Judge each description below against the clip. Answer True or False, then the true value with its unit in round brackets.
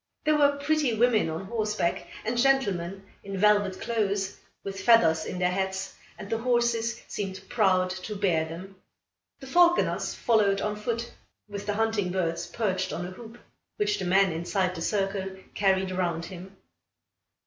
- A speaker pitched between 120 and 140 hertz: False (195 Hz)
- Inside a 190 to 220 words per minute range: False (160 wpm)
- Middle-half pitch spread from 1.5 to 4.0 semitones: True (3.5 semitones)